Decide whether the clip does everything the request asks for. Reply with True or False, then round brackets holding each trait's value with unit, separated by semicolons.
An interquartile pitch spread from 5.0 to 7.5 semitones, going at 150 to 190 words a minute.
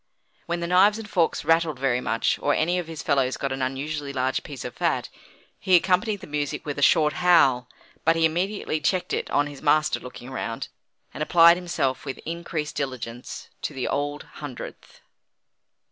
False (4.2 semitones; 180 wpm)